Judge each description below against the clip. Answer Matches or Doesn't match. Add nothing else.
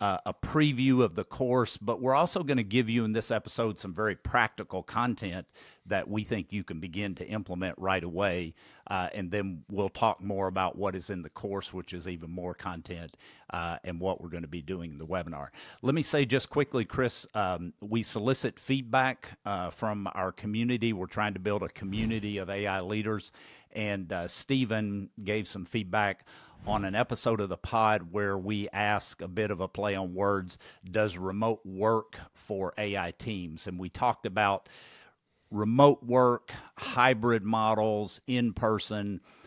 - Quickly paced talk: Doesn't match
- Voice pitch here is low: Matches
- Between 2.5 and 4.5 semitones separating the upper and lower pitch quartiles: Matches